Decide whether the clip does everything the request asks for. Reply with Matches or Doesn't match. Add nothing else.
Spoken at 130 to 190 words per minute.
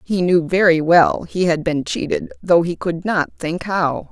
Doesn't match